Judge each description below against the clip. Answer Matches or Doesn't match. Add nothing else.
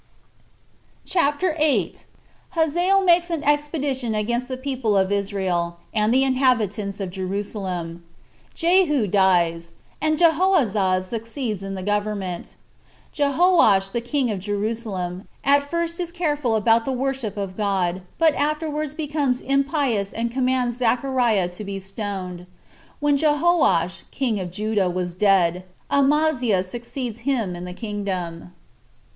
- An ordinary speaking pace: Doesn't match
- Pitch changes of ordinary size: Doesn't match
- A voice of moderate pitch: Doesn't match